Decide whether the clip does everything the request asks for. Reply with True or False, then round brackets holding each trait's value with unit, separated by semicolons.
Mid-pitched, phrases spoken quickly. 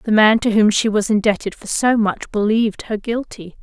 False (215 Hz; 215 wpm)